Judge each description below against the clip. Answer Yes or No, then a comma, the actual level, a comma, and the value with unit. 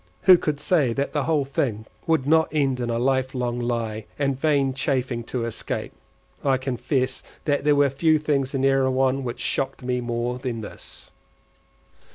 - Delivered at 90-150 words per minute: No, average, 175 wpm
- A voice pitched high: No, low, 130 Hz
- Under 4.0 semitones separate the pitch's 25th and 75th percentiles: Yes, narrow, 2.5 semitones